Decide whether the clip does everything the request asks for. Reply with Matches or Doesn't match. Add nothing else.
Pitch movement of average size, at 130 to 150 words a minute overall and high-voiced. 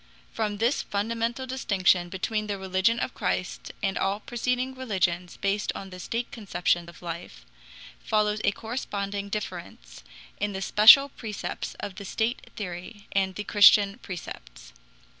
Matches